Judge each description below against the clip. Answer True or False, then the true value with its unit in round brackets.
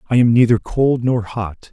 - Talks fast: True (210 wpm)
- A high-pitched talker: False (115 Hz)